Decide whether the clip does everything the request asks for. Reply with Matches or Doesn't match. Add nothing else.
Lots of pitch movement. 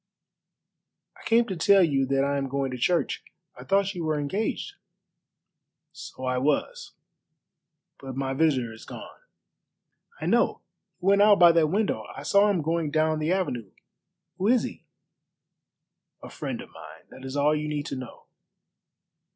Matches